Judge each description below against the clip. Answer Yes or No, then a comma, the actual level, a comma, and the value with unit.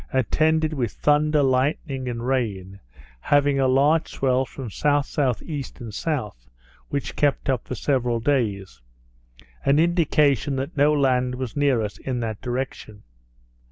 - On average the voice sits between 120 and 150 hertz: Yes, low, 135 Hz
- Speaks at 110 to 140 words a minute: Yes, slow, 135 wpm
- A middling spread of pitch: Yes, average, 3.2 semitones